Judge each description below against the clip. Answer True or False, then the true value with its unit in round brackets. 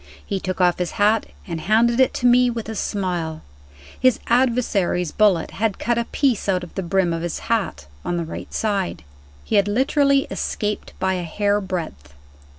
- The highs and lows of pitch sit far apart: False (4.6 semitones)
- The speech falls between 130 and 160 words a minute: False (185 wpm)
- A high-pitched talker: True (200 Hz)